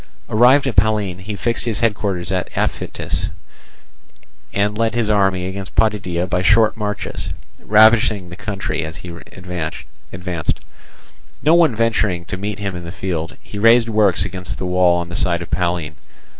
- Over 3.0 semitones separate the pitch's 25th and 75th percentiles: Yes, average, 3.4 semitones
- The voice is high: No, low, 100 Hz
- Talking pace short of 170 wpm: Yes, average, 160 wpm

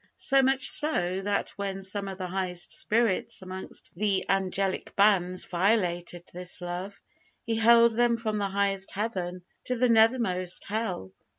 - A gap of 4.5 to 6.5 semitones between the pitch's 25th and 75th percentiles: No, average, 3.5 semitones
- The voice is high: Yes, high, 195 Hz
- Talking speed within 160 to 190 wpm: No, average, 150 wpm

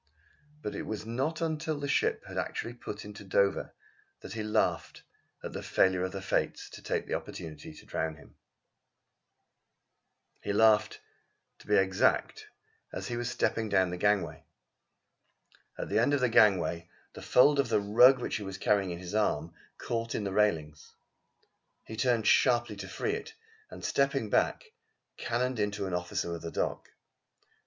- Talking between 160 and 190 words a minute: Yes, average, 170 wpm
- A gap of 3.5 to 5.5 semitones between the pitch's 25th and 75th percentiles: Yes, average, 4.3 semitones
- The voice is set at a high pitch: No, low, 105 Hz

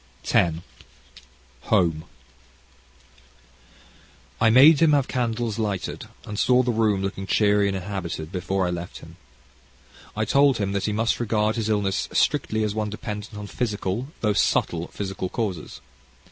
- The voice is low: Yes, low, 105 Hz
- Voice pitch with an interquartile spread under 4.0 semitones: Yes, average, 2.8 semitones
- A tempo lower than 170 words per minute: Yes, average, 145 wpm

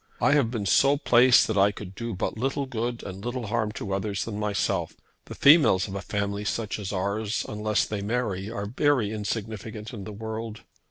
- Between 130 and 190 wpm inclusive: No, average, 200 wpm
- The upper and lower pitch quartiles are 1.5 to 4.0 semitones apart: Yes, average, 2.7 semitones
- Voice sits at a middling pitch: No, low, 110 Hz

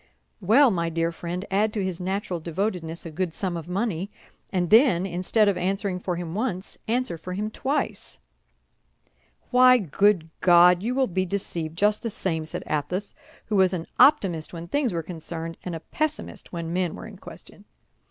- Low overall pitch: No, medium, 185 Hz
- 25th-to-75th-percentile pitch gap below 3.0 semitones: No, average, 3.6 semitones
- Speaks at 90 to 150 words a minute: No, average, 180 wpm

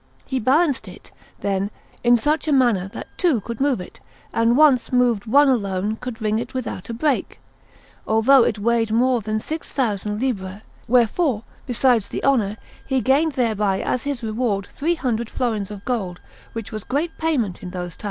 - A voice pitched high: Yes, high, 235 Hz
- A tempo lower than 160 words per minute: No, average, 175 wpm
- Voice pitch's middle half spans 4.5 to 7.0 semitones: No, average, 4.0 semitones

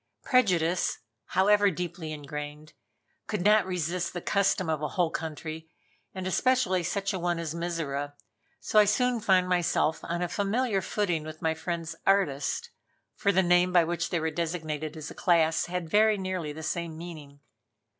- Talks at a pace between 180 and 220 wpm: No, average, 165 wpm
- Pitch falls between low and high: Yes, medium, 175 Hz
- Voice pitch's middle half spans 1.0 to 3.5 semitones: Yes, average, 3.2 semitones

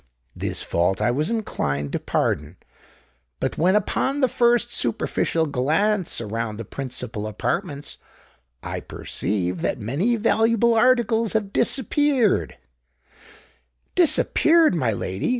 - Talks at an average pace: No, slow, 115 wpm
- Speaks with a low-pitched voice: No, medium, 160 Hz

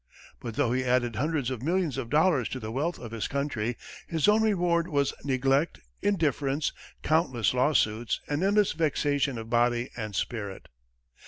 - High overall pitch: No, low, 135 Hz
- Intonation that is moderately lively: Yes, average, 4.9 semitones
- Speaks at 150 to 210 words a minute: Yes, average, 160 wpm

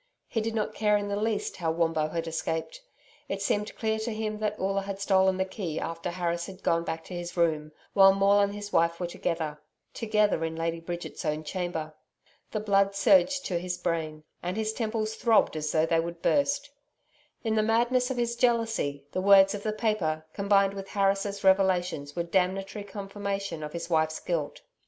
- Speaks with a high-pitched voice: Yes, high, 195 Hz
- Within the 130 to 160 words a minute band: No, average, 195 wpm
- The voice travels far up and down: No, average, 4.0 semitones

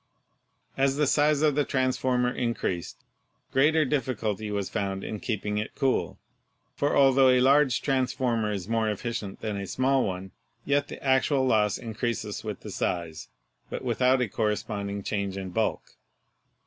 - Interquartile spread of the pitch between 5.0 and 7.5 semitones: No, average, 4.4 semitones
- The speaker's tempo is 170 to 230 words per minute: No, average, 160 wpm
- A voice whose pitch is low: Yes, low, 120 Hz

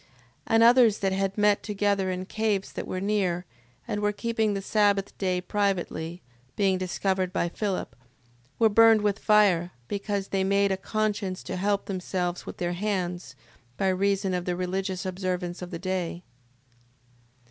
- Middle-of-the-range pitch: No, high, 195 Hz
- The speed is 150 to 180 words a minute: Yes, average, 160 wpm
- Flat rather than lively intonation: Yes, narrow, 2.1 semitones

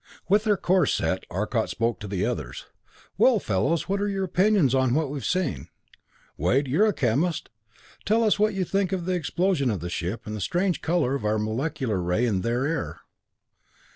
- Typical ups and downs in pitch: No, wide, 9.0 semitones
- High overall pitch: No, medium, 145 Hz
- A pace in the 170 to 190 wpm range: No, average, 200 wpm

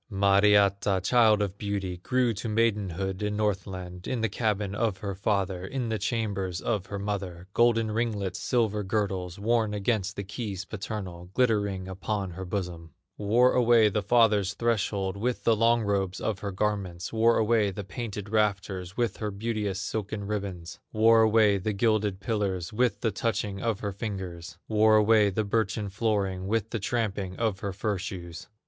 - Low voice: Yes, low, 105 Hz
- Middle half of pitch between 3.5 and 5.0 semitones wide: No, narrow, 2.5 semitones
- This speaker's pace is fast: No, average, 165 wpm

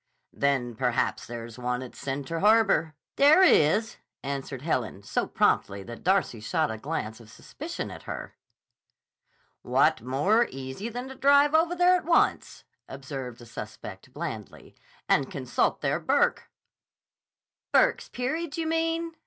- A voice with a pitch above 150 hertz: No, medium, 145 Hz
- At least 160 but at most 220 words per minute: No, average, 140 wpm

